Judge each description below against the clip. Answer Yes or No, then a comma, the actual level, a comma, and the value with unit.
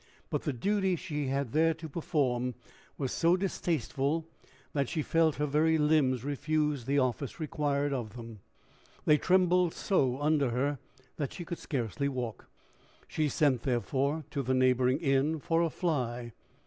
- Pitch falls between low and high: Yes, medium, 145 Hz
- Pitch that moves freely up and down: No, average, 3.7 semitones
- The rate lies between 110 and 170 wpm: Yes, average, 155 wpm